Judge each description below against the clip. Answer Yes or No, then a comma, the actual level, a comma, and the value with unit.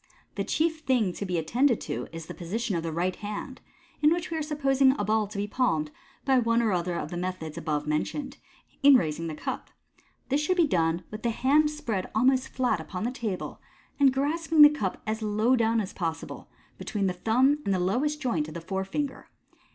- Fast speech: Yes, fast, 215 wpm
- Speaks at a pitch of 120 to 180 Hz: No, high, 220 Hz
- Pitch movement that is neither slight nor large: No, wide, 7.1 semitones